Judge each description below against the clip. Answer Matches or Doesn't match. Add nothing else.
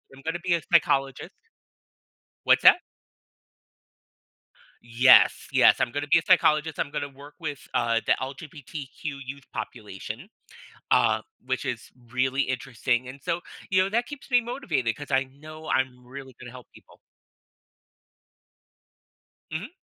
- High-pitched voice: Doesn't match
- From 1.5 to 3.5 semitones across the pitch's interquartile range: Doesn't match